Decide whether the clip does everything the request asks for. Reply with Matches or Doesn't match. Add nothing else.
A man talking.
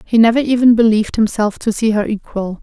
Doesn't match